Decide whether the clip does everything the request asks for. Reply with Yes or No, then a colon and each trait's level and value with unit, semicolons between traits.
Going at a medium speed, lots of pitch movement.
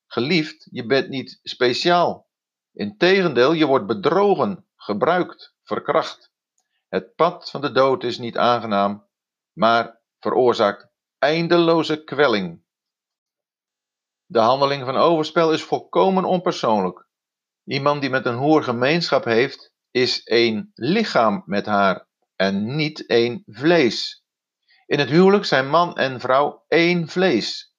No: slow, 120 wpm; wide, 6.3 semitones